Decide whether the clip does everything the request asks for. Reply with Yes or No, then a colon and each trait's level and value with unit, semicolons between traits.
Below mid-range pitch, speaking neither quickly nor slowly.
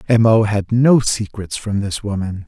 Yes: low, 105 Hz; average, 195 wpm